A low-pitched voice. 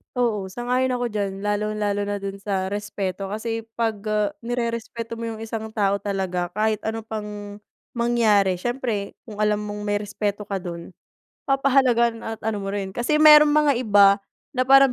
No: high, 215 Hz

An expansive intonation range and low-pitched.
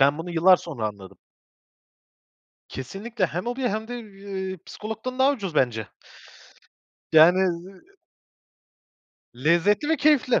No: wide, 5.8 semitones; high, 190 Hz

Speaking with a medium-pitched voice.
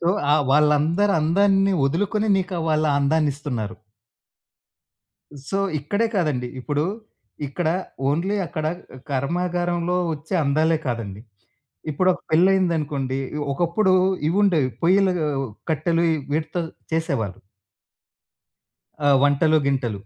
Yes: medium, 160 Hz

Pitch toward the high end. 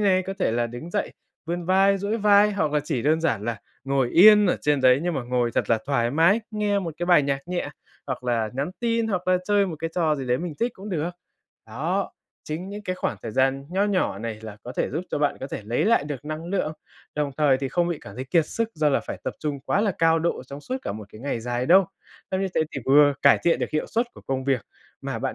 No: medium, 155 Hz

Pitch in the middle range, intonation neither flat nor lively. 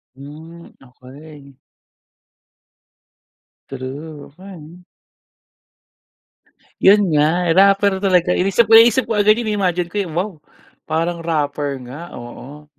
Yes: medium, 165 Hz; average, 5.0 semitones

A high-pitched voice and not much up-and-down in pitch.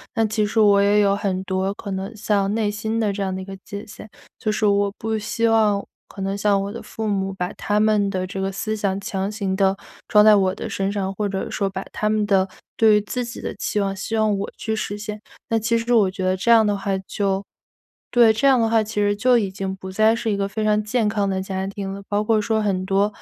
Yes: high, 205 Hz; narrow, 1.8 semitones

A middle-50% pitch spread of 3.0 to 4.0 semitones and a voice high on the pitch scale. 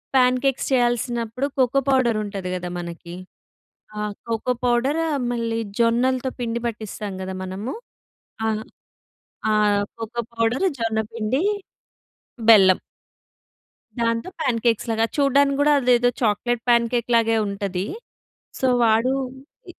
No: narrow, 2.5 semitones; high, 230 Hz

